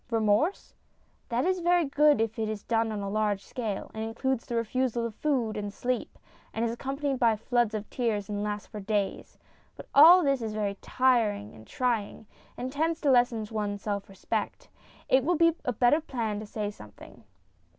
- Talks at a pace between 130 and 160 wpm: No, average, 180 wpm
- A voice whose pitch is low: No, high, 230 Hz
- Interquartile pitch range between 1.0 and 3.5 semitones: No, average, 3.9 semitones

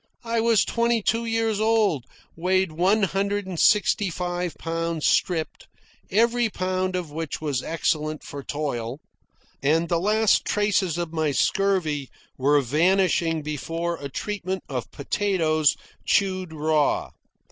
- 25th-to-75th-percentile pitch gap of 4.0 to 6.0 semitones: Yes, average, 4.5 semitones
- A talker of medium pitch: Yes, medium, 175 Hz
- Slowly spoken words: Yes, slow, 130 wpm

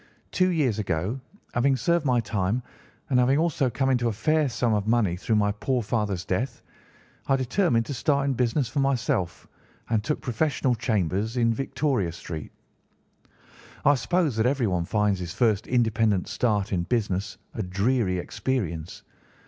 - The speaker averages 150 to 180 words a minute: Yes, average, 155 wpm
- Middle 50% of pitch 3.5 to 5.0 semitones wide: Yes, average, 4.6 semitones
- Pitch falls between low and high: No, low, 115 Hz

